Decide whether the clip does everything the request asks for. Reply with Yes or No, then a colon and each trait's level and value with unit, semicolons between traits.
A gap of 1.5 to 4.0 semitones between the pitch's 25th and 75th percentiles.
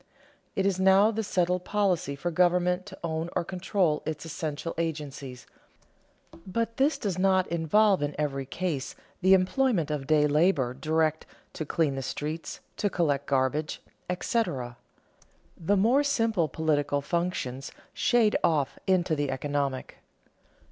No: average, 4.5 semitones